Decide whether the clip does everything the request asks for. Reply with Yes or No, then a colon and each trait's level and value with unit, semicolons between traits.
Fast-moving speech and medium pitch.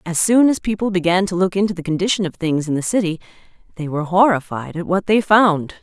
Yes: fast, 225 wpm; medium, 180 Hz